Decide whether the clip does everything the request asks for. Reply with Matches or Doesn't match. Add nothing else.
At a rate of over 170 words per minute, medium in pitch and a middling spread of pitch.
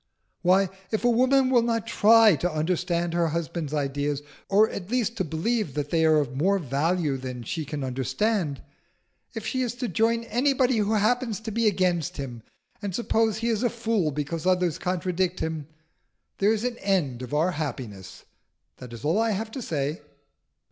Doesn't match